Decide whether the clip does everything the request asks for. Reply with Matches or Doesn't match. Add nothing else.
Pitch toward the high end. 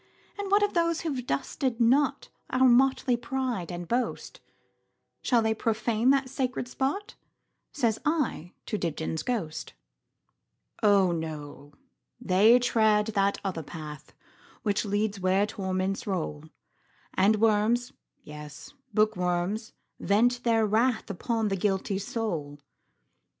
Matches